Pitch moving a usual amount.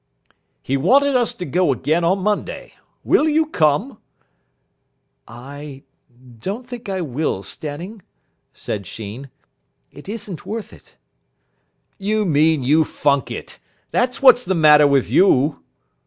No: wide, 7.2 semitones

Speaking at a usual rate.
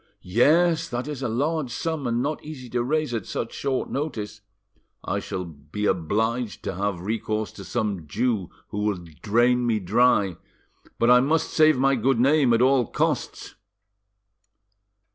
Yes: average, 160 wpm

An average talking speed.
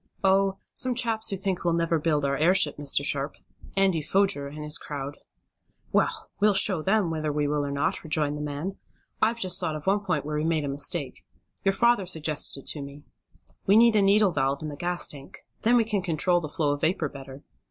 No: fast, 215 wpm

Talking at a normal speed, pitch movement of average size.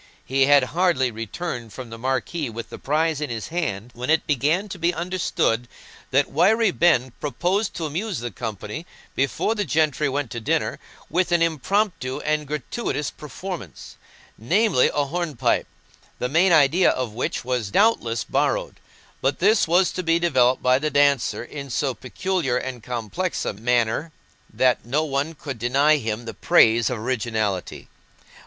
No: average, 160 wpm; wide, 5.7 semitones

